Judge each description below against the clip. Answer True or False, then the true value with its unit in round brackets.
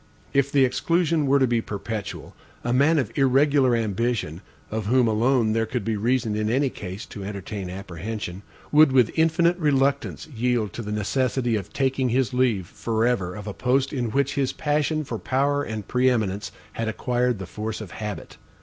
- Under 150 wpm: False (180 wpm)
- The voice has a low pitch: True (120 Hz)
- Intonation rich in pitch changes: False (4.1 semitones)